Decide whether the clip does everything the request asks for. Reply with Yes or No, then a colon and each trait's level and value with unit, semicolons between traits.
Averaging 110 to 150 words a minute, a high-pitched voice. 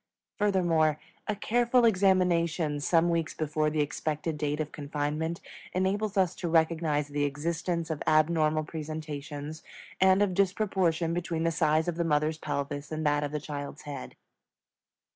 No: average, 145 wpm; medium, 160 Hz